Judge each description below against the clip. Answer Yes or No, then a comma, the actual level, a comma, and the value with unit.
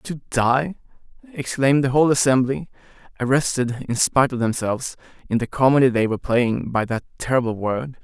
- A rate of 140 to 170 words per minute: Yes, average, 155 wpm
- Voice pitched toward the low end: Yes, low, 130 Hz